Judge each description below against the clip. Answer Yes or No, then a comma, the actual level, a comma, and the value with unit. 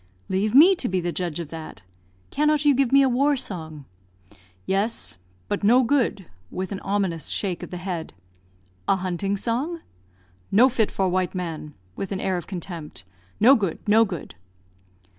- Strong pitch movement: Yes, wide, 5.7 semitones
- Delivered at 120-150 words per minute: No, average, 170 wpm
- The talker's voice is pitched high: Yes, high, 195 Hz